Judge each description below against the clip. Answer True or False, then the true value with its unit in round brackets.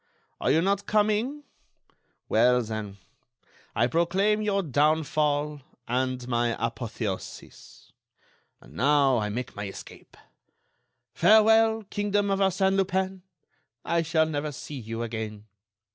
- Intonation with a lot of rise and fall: True (8.6 semitones)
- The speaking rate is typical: False (115 wpm)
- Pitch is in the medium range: True (150 Hz)